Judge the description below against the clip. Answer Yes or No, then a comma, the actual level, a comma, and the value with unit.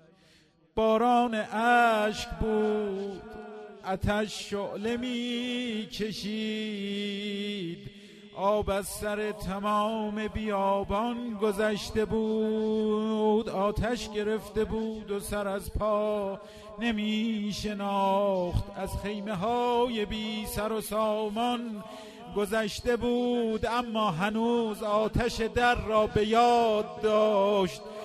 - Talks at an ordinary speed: No, slow, 85 wpm